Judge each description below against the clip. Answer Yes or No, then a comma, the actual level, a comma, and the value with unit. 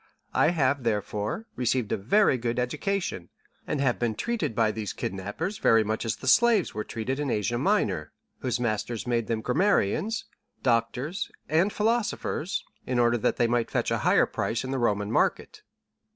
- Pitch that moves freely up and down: Yes, wide, 6.2 semitones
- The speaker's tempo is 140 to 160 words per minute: No, average, 170 wpm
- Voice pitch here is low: Yes, low, 120 Hz